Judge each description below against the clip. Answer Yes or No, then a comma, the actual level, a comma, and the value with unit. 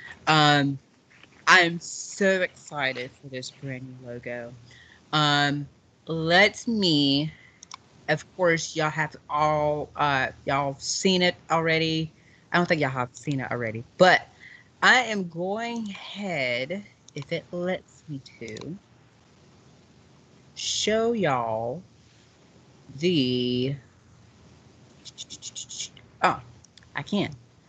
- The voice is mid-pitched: Yes, medium, 145 Hz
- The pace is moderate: No, slow, 100 wpm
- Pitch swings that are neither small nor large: Yes, average, 5.0 semitones